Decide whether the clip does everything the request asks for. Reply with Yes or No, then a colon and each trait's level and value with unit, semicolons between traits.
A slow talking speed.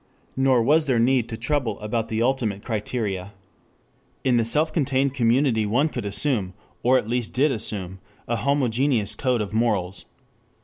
No: average, 160 wpm